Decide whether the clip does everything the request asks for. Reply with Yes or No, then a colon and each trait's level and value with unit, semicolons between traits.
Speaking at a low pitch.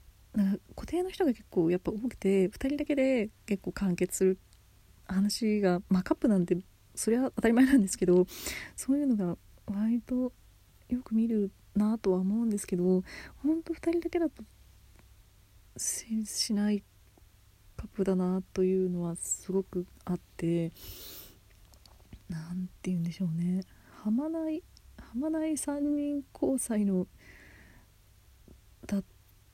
No: high, 190 Hz